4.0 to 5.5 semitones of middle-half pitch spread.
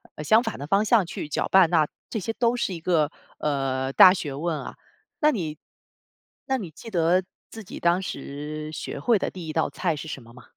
Yes: average, 4.5 semitones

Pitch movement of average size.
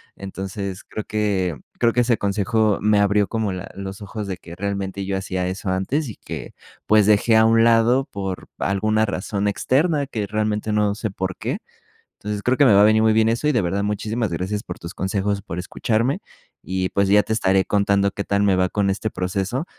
No: narrow, 2.2 semitones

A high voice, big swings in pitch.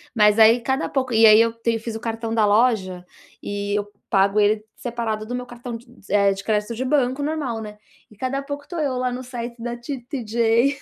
No: high, 230 Hz; average, 2.8 semitones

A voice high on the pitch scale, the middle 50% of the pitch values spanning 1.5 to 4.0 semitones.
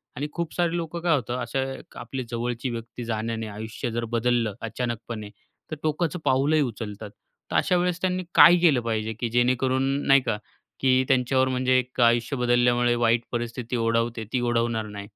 No: low, 120 Hz; narrow, 2.5 semitones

